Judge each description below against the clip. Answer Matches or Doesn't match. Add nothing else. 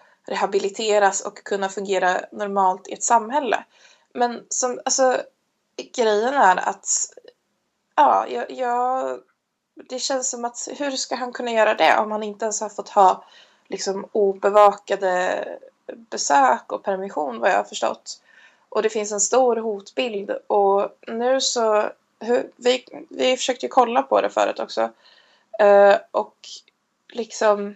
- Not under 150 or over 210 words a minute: Doesn't match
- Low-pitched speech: Doesn't match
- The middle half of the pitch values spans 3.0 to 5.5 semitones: Matches